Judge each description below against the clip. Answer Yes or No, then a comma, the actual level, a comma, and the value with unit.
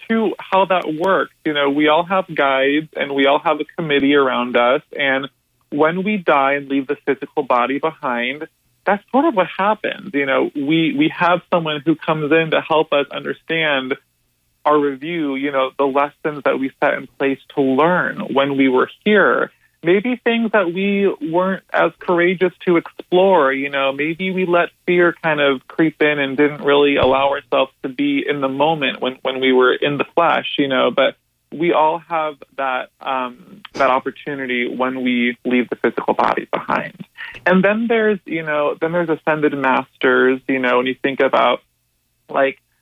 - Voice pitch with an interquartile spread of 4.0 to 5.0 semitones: Yes, average, 4.7 semitones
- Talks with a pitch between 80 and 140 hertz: No, medium, 150 Hz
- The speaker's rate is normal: Yes, average, 185 wpm